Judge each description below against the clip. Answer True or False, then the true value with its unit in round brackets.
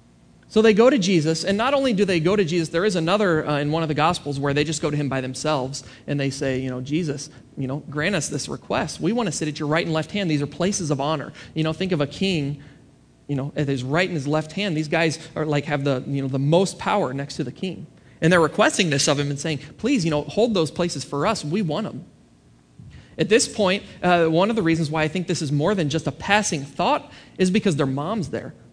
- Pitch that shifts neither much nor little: True (4.1 semitones)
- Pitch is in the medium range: True (155 Hz)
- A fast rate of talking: True (270 wpm)